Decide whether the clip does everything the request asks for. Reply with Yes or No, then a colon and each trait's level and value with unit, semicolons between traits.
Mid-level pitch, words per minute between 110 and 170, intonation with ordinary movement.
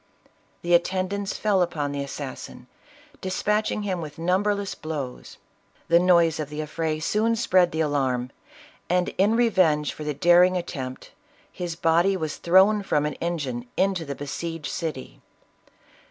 Yes: medium, 170 Hz; average, 145 wpm; average, 3.9 semitones